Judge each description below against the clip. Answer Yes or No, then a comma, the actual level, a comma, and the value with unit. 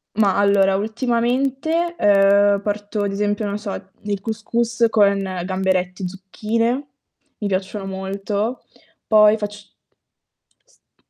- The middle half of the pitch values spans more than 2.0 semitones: Yes, narrow, 2.5 semitones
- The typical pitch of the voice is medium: No, high, 205 Hz